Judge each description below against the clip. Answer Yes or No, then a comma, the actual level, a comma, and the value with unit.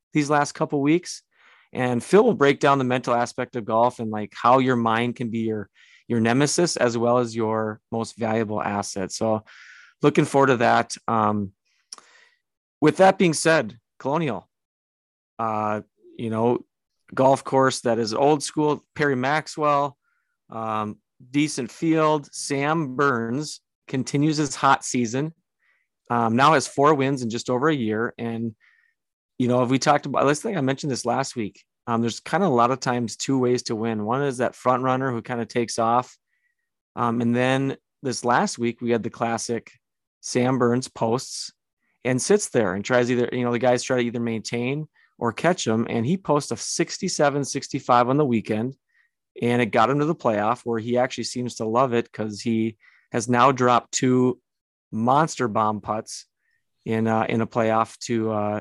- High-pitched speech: No, low, 125 Hz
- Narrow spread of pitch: No, average, 3.6 semitones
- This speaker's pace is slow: No, average, 180 wpm